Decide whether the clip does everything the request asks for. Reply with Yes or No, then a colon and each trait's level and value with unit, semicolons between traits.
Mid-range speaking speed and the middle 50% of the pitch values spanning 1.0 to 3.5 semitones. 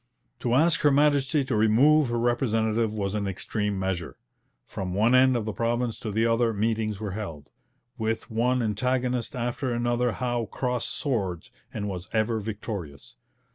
Yes: average, 160 wpm; average, 2.9 semitones